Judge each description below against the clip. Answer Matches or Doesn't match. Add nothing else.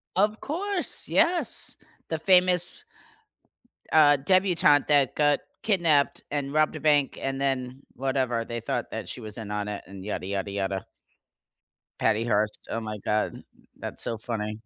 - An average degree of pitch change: Doesn't match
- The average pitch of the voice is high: Doesn't match